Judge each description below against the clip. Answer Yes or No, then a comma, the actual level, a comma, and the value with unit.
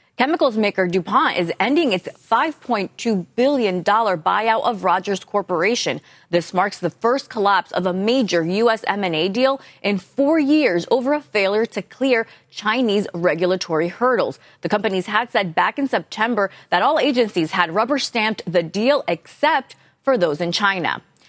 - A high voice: Yes, high, 210 Hz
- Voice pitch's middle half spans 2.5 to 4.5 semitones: No, average, 5.0 semitones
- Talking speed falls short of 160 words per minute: Yes, average, 150 wpm